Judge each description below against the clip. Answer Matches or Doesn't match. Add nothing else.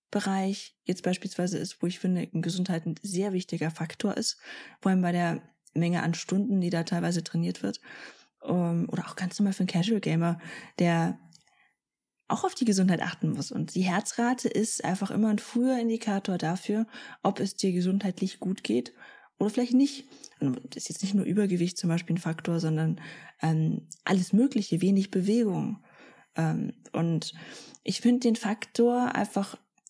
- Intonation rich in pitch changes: Doesn't match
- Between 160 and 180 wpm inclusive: Matches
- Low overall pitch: Doesn't match